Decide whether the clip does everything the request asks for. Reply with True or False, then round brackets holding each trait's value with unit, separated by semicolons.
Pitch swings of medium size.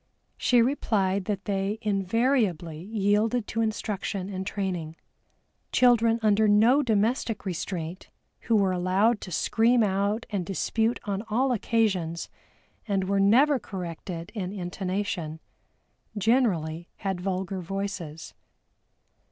True (3.4 semitones)